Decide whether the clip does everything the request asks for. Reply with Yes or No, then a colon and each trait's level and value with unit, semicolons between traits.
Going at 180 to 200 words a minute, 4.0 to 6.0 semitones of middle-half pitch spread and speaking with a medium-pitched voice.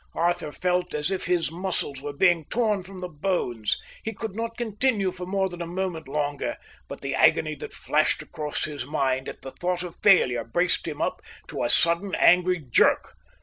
Yes: average, 190 wpm; average, 4.3 semitones; medium, 175 Hz